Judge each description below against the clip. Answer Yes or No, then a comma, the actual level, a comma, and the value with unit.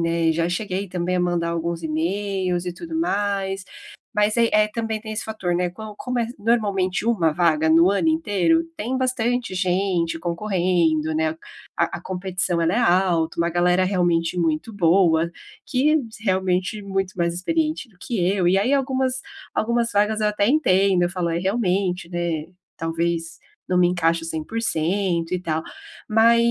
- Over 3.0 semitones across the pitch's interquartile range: Yes, average, 3.9 semitones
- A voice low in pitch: No, medium, 185 Hz